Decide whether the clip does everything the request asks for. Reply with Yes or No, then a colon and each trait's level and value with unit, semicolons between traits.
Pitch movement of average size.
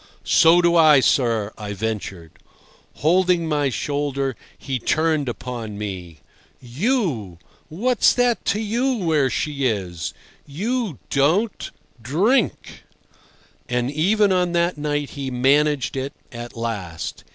No: wide, 6.8 semitones